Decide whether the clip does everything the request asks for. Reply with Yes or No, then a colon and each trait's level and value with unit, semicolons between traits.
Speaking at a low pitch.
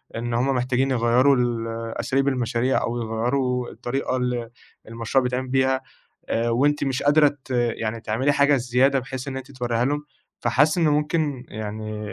Yes: low, 125 Hz